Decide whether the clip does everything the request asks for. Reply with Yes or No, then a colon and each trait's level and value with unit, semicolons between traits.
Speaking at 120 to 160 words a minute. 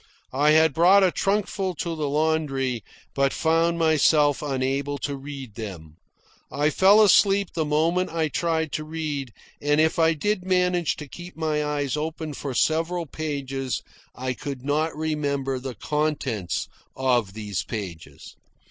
Yes: average, 150 wpm